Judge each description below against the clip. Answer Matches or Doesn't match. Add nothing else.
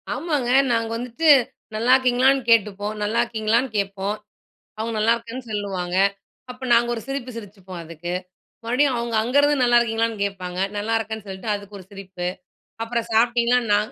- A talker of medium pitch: Doesn't match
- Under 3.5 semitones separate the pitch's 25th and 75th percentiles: Matches